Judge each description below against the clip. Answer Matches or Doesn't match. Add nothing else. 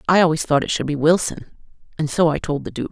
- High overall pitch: Doesn't match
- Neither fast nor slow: Doesn't match